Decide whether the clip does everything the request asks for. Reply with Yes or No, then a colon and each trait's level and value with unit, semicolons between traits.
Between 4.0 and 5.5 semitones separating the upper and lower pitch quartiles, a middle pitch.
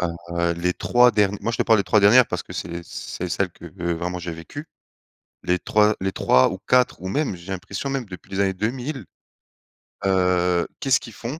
No: average, 4.7 semitones; very low, 95 Hz